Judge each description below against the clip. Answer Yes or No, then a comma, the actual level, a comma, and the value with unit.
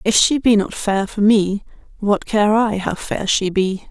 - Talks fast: Yes, fast, 215 wpm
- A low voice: No, high, 205 Hz